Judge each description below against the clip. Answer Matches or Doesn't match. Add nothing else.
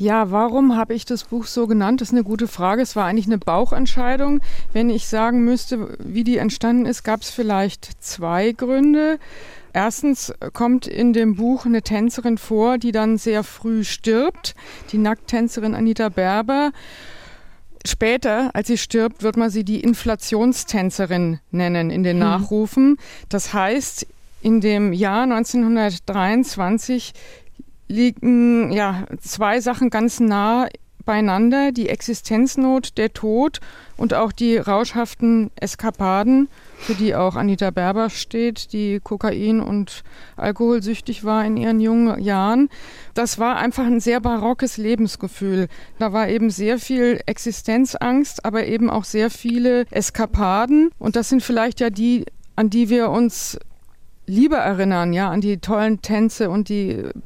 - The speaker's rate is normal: Matches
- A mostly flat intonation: Matches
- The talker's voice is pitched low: Doesn't match